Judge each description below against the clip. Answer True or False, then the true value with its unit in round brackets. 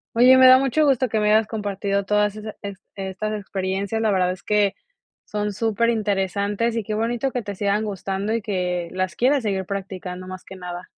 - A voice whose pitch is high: True (205 Hz)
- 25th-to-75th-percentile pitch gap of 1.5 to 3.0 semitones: True (2.6 semitones)